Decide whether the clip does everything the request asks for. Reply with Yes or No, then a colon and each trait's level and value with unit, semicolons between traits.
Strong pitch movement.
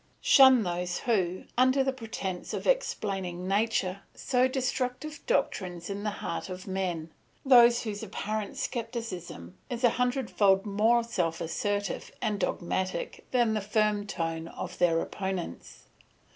No: average, 4.8 semitones